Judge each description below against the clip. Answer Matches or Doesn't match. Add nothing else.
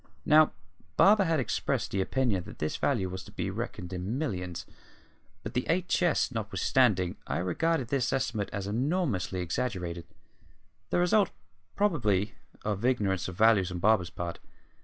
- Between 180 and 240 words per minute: Doesn't match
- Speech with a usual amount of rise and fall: Doesn't match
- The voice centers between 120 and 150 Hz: Doesn't match